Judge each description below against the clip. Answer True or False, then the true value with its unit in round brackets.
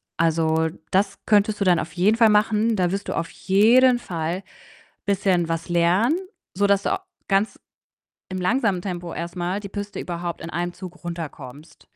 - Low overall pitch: False (185 Hz)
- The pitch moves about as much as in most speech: True (3.2 semitones)